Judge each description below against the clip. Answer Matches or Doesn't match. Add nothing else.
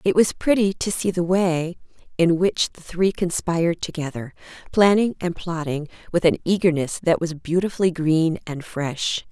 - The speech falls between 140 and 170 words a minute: Matches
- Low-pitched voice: Doesn't match